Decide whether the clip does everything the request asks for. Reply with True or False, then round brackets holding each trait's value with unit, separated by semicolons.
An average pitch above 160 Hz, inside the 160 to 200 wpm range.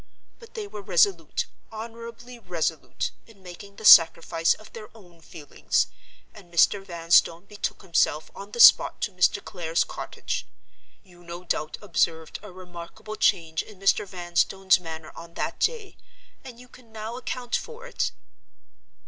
False (190 Hz; 145 wpm)